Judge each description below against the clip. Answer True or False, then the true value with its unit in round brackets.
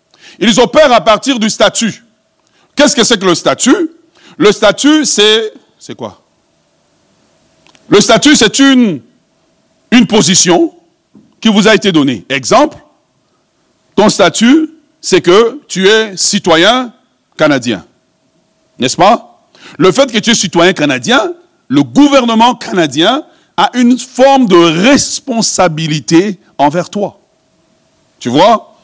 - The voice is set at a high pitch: True (230 Hz)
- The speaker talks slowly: True (120 wpm)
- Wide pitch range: True (6.2 semitones)